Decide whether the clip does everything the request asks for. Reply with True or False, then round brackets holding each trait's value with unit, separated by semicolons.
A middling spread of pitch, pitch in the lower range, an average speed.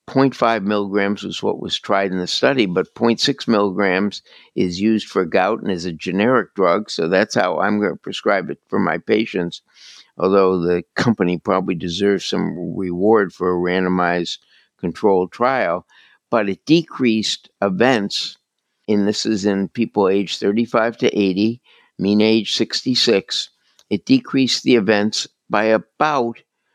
True (3.3 semitones; 100 Hz; 150 wpm)